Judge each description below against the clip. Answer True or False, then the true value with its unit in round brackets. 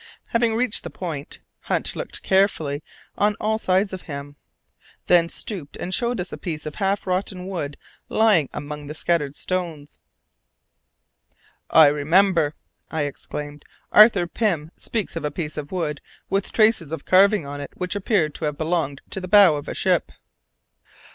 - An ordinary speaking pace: True (160 wpm)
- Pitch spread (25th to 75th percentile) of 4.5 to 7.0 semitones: True (4.8 semitones)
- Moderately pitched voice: True (170 Hz)